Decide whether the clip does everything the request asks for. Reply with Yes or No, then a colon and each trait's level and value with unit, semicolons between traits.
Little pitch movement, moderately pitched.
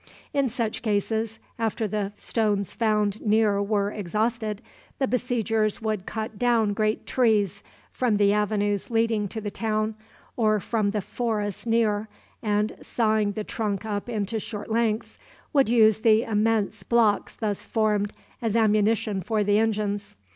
No: narrow, 1.6 semitones; high, 215 Hz